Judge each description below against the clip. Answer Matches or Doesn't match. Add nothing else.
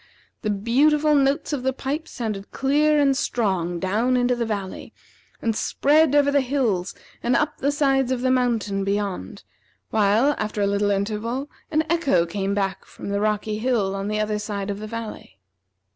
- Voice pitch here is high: Matches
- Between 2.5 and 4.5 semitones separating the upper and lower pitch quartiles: Doesn't match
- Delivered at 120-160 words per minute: Doesn't match